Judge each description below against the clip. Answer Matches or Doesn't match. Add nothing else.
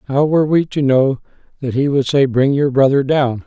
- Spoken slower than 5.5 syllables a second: Matches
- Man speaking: Matches